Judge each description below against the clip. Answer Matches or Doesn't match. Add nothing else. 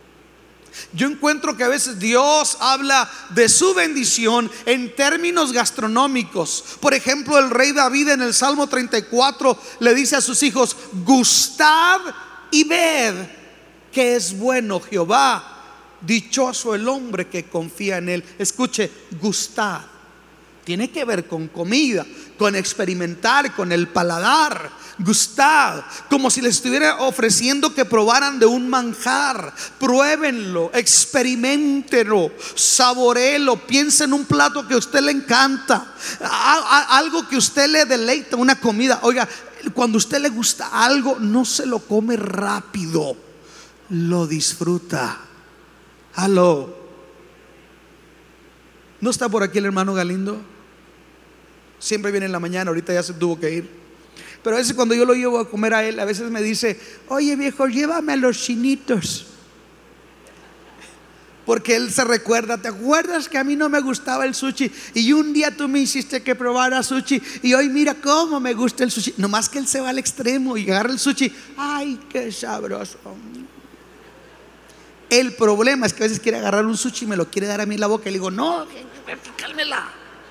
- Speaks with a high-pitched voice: Matches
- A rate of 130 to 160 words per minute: Matches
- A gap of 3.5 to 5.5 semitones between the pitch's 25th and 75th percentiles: Matches